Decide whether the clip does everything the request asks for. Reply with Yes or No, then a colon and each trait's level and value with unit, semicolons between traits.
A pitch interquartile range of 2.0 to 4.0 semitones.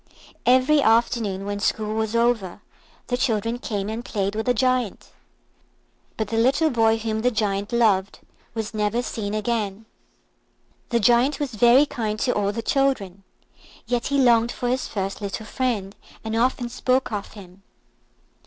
Yes: average, 3.0 semitones